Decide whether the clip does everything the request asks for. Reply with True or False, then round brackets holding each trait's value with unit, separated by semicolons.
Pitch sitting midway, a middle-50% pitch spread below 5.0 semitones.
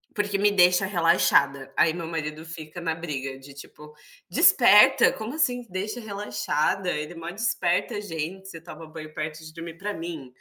True (170 Hz; 4.1 semitones)